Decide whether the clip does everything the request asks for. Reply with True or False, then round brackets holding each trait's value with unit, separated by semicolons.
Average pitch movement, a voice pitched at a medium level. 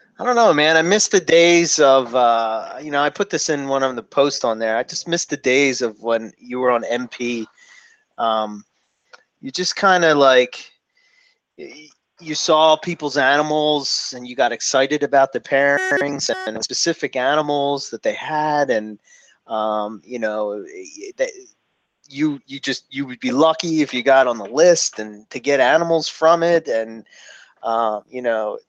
False (5.8 semitones; 145 Hz)